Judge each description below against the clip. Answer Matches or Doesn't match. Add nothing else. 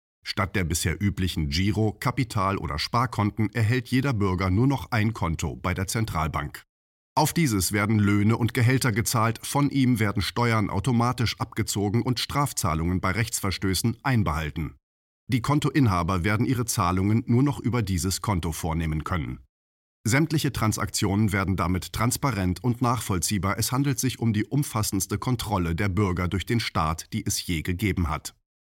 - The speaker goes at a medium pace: Matches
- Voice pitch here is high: Doesn't match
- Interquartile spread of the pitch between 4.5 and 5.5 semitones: Matches